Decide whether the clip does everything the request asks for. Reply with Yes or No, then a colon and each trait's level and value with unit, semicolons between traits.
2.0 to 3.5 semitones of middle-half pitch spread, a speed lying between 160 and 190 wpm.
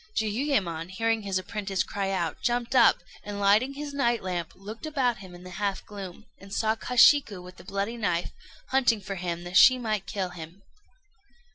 No: average, 4.1 semitones; average, 180 wpm